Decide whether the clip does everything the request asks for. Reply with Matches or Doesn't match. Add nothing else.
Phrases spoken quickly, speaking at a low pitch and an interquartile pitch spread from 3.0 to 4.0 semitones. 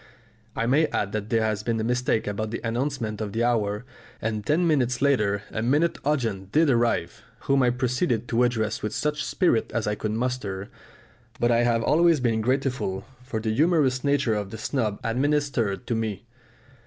Doesn't match